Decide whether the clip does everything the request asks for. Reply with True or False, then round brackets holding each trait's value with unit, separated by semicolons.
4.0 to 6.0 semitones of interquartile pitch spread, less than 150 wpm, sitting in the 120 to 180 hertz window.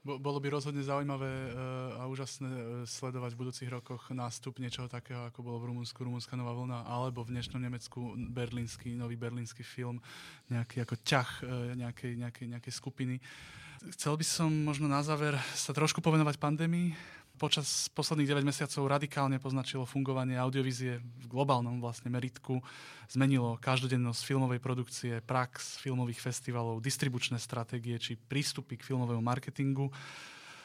False (2.5 semitones; 140 wpm; 130 Hz)